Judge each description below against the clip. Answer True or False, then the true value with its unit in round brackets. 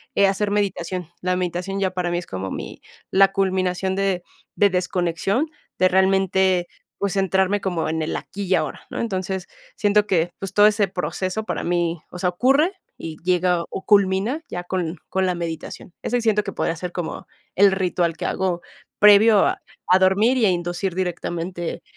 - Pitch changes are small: True (2.0 semitones)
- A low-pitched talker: False (185 Hz)